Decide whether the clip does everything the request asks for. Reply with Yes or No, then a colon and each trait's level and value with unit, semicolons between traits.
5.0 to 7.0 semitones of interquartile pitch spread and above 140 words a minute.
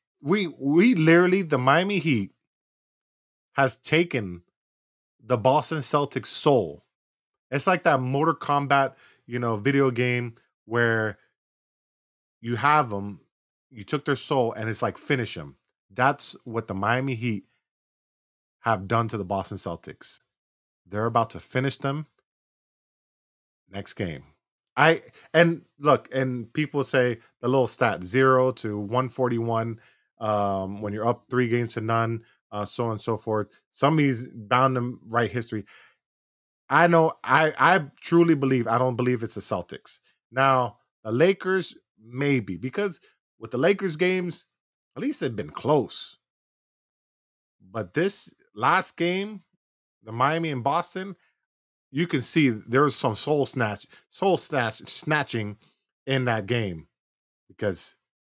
No: average, 5.3 semitones; slow, 135 wpm